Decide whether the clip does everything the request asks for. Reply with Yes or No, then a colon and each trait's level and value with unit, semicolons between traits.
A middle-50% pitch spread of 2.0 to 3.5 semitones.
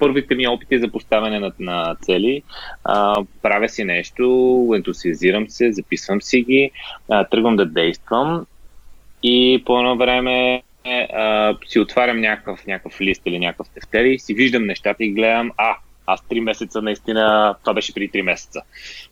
Yes: average, 3.1 semitones